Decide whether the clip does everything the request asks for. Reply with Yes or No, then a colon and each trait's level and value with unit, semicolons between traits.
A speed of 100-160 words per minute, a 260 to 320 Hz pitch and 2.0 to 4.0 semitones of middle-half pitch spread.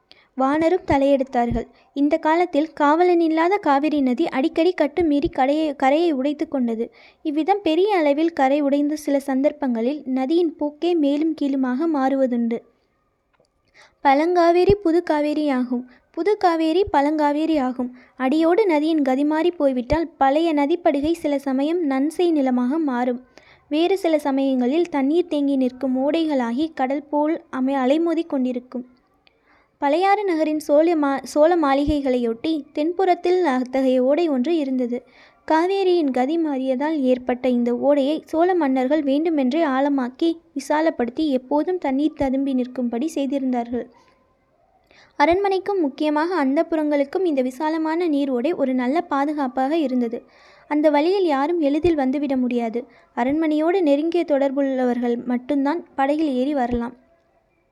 Yes: average, 110 wpm; very high, 290 Hz; average, 3.4 semitones